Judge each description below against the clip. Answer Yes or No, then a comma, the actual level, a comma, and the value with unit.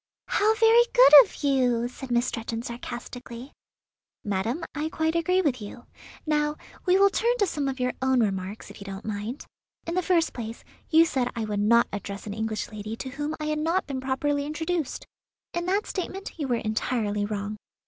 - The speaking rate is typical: Yes, average, 190 wpm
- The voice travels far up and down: Yes, wide, 6.5 semitones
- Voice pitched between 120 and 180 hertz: No, very high, 260 Hz